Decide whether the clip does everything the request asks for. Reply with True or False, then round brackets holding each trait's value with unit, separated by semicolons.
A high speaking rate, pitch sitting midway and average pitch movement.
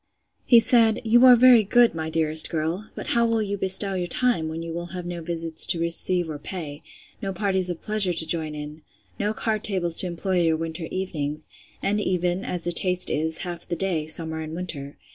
True (210 wpm; 175 Hz; 3.5 semitones)